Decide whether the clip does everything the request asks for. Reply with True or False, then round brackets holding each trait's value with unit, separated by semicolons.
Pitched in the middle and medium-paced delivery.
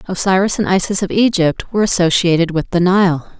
True (180 Hz; 175 wpm)